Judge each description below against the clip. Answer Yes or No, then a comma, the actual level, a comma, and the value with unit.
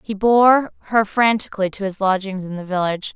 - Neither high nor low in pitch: No, high, 205 Hz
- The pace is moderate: Yes, average, 190 wpm